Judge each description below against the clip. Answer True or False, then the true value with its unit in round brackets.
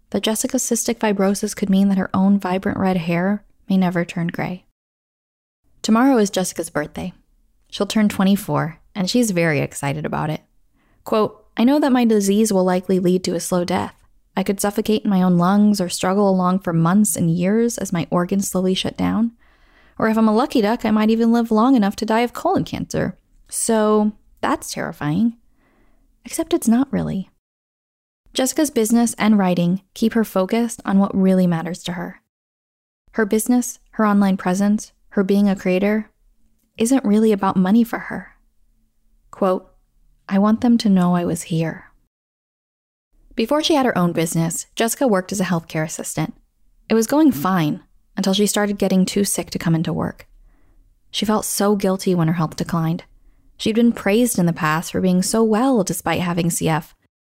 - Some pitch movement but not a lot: True (3.7 semitones)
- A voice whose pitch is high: True (200 Hz)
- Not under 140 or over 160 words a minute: False (180 wpm)